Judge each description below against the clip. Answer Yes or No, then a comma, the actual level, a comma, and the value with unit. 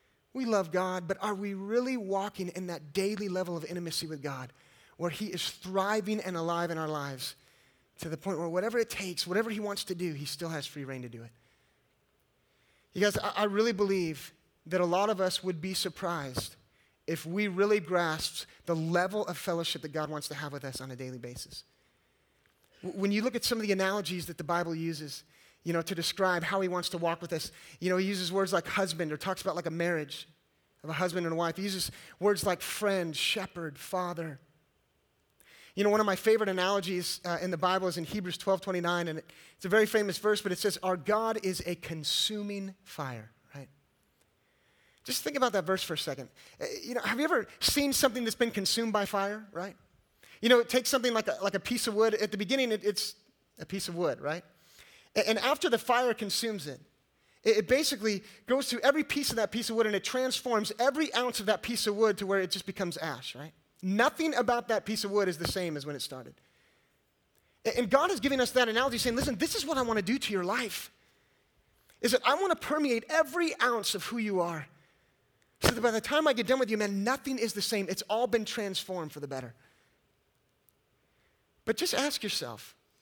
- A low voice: No, high, 195 Hz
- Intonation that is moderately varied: Yes, average, 4.6 semitones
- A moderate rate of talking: No, fast, 220 wpm